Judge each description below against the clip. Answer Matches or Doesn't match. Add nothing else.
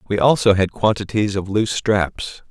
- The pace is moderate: Matches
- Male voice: Matches